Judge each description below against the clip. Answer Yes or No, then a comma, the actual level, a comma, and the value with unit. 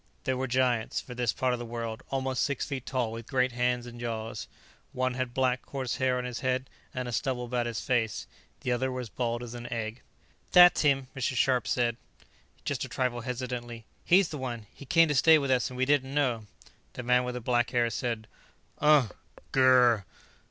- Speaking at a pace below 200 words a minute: No, fast, 205 wpm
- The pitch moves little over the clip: Yes, narrow, 1.6 semitones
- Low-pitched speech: Yes, low, 125 Hz